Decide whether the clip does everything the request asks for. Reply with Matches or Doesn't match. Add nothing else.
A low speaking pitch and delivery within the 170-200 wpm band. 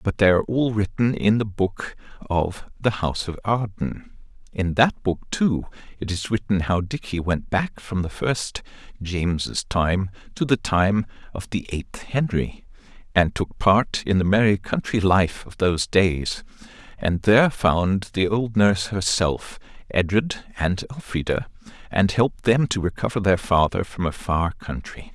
Doesn't match